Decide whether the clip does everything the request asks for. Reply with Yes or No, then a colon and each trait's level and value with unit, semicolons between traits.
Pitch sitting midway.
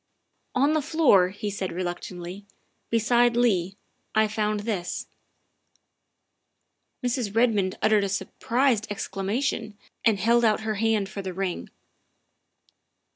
No: high, 210 Hz